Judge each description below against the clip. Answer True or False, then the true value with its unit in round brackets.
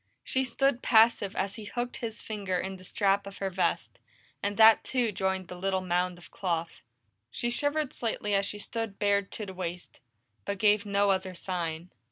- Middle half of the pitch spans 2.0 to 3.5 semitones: True (3.0 semitones)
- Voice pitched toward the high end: True (200 Hz)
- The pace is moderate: True (190 wpm)